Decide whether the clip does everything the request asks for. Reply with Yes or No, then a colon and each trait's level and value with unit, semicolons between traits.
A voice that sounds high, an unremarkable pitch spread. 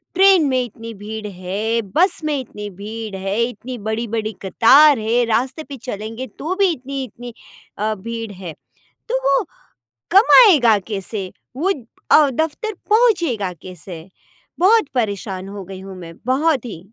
No: high, 230 Hz; wide, 5.8 semitones